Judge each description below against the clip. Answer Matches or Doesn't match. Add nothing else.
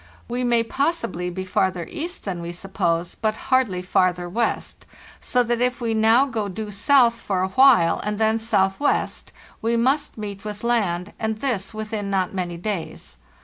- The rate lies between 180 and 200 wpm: Doesn't match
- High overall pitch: Matches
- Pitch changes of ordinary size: Matches